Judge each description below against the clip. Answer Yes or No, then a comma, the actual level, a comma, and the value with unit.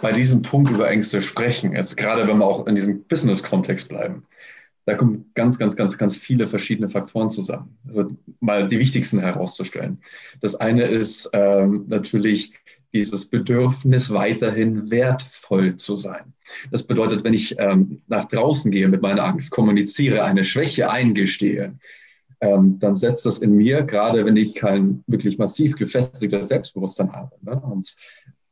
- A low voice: Yes, low, 105 Hz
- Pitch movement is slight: No, average, 3.1 semitones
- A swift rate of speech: No, average, 155 wpm